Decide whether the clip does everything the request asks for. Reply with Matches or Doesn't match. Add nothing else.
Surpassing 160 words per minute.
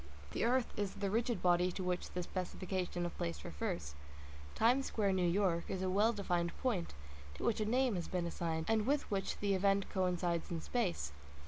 Matches